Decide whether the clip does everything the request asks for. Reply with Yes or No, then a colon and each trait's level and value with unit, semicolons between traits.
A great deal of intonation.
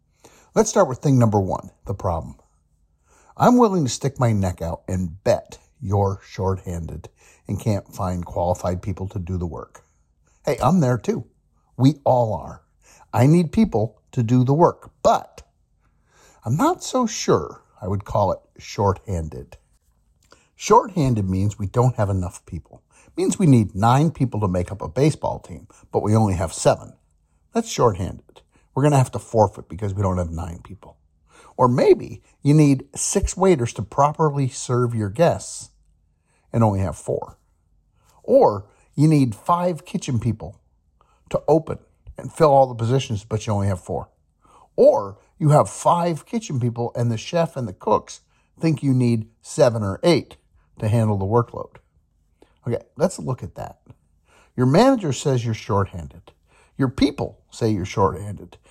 Yes: wide, 7.0 semitones